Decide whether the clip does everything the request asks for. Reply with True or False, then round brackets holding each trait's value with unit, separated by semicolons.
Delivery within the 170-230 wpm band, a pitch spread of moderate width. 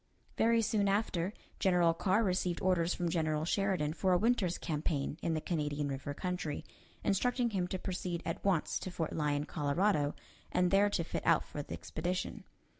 True (175 wpm; 3.7 semitones)